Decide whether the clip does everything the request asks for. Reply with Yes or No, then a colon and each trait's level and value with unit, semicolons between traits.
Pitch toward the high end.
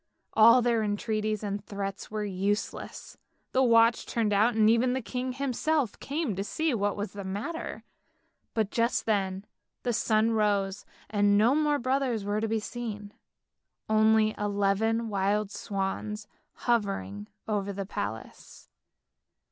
Yes: high, 215 Hz